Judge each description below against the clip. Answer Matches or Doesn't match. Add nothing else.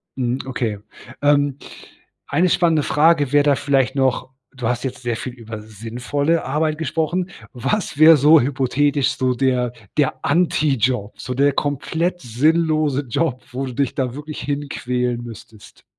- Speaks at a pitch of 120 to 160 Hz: Matches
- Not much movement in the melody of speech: Doesn't match